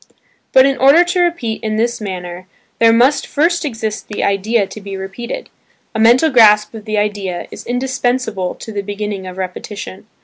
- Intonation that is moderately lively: Yes, average, 3.9 semitones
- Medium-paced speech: Yes, average, 175 wpm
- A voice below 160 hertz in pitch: No, high, 220 Hz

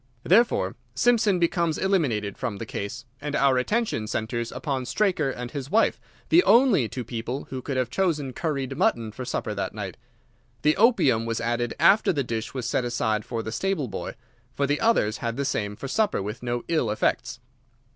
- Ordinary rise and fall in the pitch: No, wide, 6.2 semitones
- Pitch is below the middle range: Yes, low, 130 Hz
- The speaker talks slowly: No, average, 185 wpm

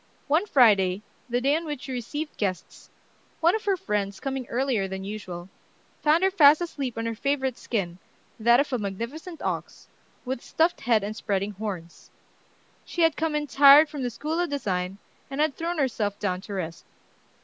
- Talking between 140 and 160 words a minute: No, average, 180 wpm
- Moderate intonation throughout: No, wide, 6.8 semitones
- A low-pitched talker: No, very high, 250 Hz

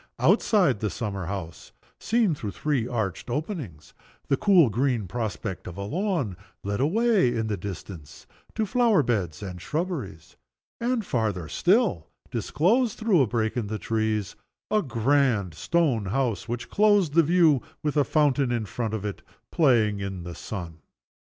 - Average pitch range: No, wide, 8.5 semitones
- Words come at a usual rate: Yes, average, 155 wpm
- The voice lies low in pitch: Yes, low, 120 Hz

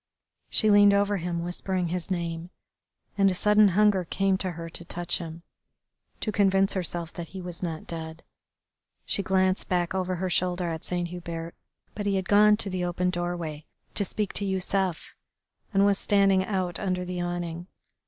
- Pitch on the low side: No, medium, 180 Hz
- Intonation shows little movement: Yes, narrow, 2.1 semitones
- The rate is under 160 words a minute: No, average, 175 wpm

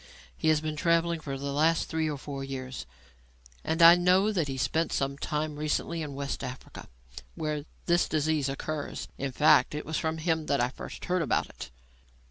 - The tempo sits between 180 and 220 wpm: Yes, average, 190 wpm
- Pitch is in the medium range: Yes, medium, 155 Hz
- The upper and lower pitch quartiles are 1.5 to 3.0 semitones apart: Yes, average, 2.7 semitones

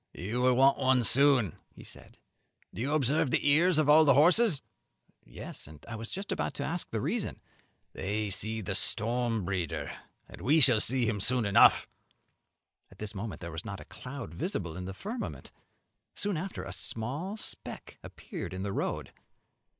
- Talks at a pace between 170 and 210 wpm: Yes, average, 175 wpm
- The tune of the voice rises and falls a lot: Yes, wide, 6.6 semitones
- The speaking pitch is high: No, low, 125 Hz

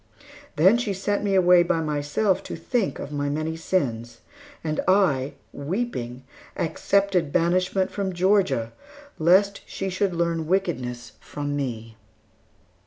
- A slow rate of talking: Yes, slow, 125 wpm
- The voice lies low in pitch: No, medium, 170 Hz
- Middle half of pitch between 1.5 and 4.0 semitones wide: No, average, 5.1 semitones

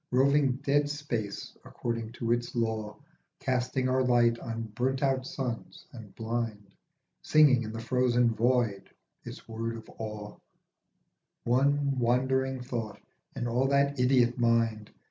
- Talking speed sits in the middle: No, slow, 130 wpm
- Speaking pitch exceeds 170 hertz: No, low, 120 Hz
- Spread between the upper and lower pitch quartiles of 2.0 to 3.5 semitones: Yes, narrow, 2.4 semitones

